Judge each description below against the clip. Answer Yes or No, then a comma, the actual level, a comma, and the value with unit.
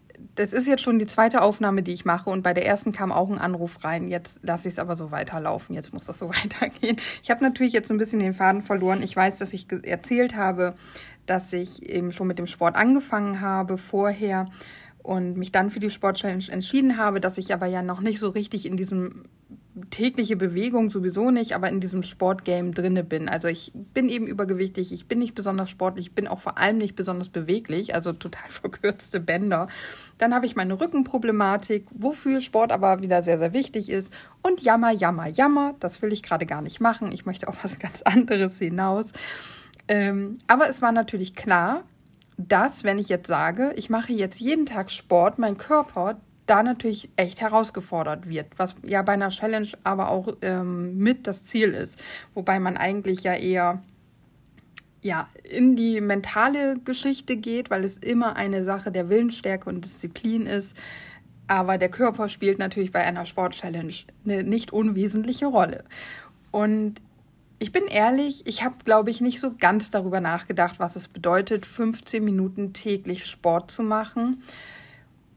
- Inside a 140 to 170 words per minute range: No, average, 180 wpm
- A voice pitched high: Yes, high, 200 Hz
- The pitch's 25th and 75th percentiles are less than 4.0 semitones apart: Yes, average, 3.4 semitones